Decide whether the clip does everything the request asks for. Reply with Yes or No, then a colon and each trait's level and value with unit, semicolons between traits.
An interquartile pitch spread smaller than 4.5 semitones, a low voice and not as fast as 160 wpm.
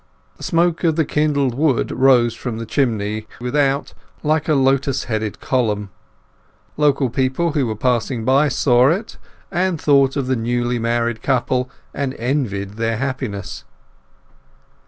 Yes: average, 3.5 semitones; low, 130 Hz; average, 140 wpm